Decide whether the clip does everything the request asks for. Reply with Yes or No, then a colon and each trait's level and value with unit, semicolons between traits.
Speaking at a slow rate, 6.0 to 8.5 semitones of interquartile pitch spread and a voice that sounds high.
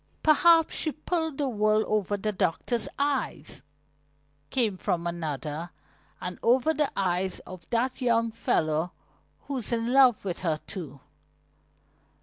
Yes: slow, 130 wpm; wide, 7.0 semitones; high, 215 Hz